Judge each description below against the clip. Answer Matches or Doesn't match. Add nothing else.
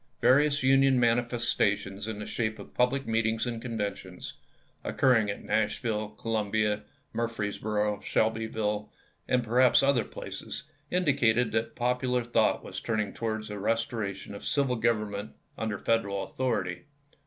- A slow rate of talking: Matches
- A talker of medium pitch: Doesn't match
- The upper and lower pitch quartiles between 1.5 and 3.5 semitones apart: Matches